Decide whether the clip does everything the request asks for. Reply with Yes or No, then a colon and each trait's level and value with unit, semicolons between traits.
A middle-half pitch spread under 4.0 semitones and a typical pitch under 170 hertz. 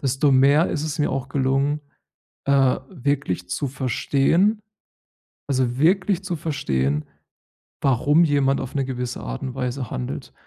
Yes: average, 2.7 semitones; low, 135 Hz